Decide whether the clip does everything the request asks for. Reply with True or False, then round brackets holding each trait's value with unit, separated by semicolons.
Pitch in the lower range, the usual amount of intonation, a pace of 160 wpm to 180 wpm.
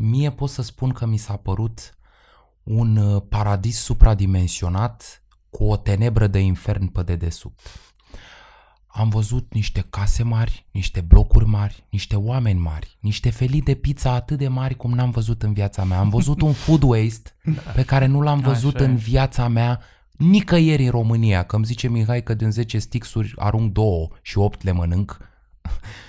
True (110 Hz; 3.7 semitones; 165 wpm)